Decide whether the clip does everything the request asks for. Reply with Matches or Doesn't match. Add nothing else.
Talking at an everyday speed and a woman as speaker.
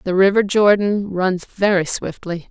Matches